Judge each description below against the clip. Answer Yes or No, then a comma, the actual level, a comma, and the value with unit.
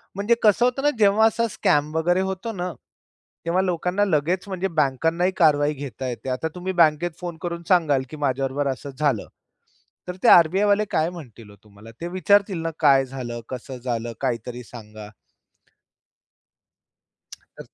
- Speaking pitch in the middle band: Yes, medium, 160 Hz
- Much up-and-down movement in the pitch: Yes, wide, 5.8 semitones